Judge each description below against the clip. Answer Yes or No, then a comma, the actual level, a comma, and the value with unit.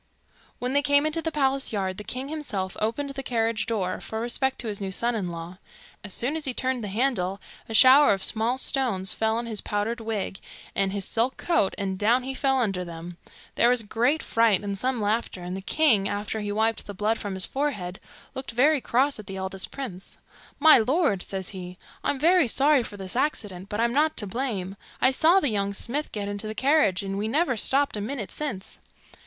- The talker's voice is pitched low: No, high, 225 Hz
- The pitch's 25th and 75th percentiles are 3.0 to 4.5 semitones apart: No, average, 5.2 semitones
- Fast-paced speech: Yes, fast, 215 wpm